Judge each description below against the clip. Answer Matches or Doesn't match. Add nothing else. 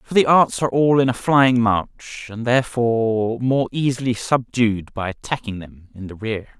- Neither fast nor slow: Matches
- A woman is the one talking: Doesn't match